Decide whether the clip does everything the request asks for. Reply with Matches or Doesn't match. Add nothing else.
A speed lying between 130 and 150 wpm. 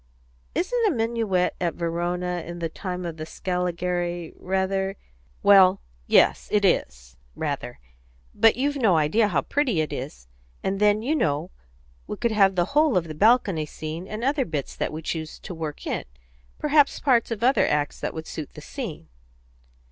Doesn't match